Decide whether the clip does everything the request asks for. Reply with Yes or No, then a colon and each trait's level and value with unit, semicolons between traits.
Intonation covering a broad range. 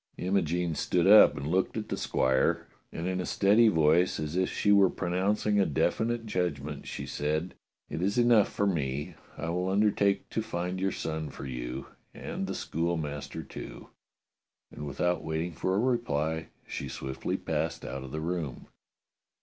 No: average, 4.5 semitones